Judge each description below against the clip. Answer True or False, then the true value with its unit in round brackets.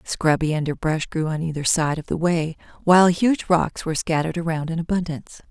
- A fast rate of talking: False (195 wpm)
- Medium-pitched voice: True (165 Hz)